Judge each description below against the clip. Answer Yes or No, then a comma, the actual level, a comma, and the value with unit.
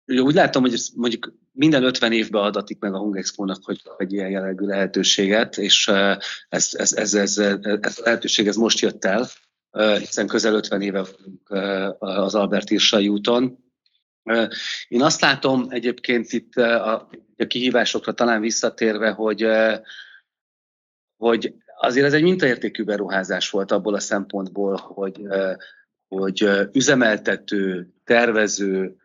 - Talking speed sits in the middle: Yes, average, 130 wpm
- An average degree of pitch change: Yes, average, 3.0 semitones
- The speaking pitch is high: No, low, 105 Hz